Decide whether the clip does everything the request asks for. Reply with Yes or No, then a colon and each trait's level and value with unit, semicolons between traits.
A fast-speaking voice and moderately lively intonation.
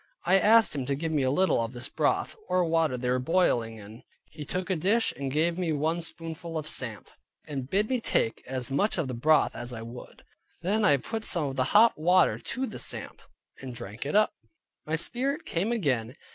No: fast, 220 wpm; wide, 6.5 semitones